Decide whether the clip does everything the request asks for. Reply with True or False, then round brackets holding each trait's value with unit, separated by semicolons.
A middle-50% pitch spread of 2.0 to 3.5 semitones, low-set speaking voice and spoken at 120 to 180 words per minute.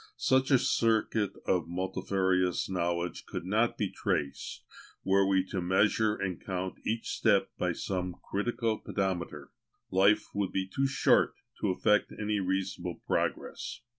True (2.6 semitones; 95 Hz; 135 wpm)